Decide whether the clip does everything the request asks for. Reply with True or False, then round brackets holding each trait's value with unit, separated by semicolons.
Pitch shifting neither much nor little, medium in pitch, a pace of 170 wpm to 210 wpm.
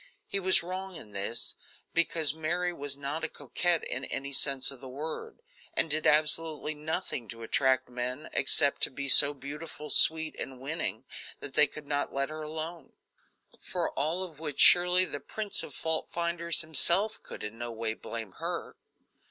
True (3.6 semitones; 150 Hz; 175 wpm)